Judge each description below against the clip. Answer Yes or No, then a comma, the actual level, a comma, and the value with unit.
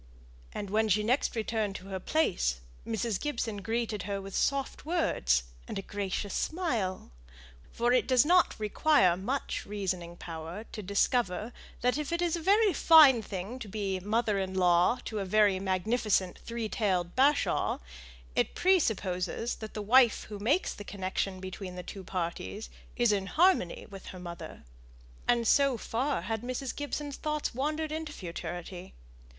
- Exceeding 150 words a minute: Yes, average, 160 wpm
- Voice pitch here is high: Yes, high, 215 Hz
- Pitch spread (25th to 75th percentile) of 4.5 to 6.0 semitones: Yes, wide, 5.5 semitones